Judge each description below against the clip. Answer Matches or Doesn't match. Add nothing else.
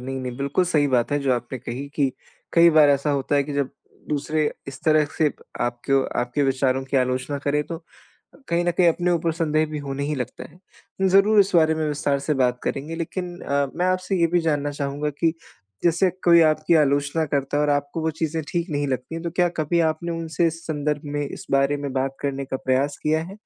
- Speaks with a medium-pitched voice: Matches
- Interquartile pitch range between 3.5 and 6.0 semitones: Doesn't match